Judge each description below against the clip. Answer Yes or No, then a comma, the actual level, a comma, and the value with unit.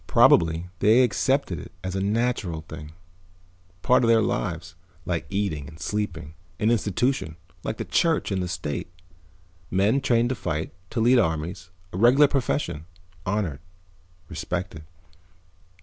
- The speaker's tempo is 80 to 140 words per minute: Yes, slow, 135 wpm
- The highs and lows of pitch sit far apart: Yes, wide, 6.4 semitones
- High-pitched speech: No, very low, 95 Hz